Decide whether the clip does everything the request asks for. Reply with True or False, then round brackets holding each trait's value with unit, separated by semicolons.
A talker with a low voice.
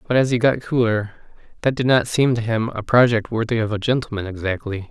True (115 Hz)